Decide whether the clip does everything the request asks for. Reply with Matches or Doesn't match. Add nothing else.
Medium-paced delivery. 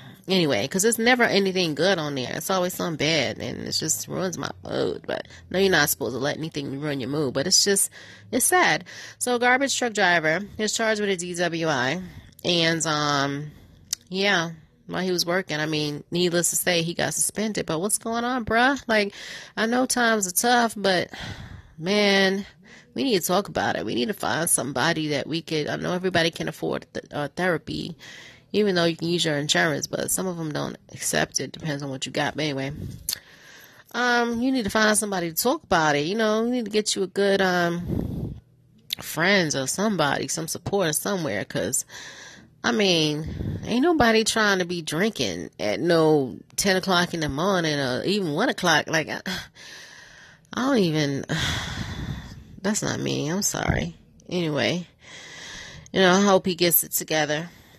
Matches